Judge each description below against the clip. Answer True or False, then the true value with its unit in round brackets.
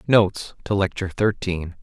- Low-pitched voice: True (100 Hz)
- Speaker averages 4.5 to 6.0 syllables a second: True (5.3 syllables/s)